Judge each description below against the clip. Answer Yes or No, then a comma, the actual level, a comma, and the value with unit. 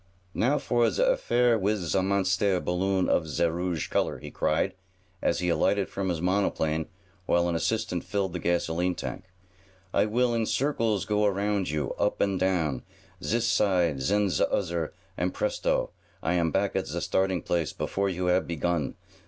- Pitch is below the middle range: Yes, very low, 95 Hz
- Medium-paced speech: Yes, average, 170 wpm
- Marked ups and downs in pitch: No, average, 3.4 semitones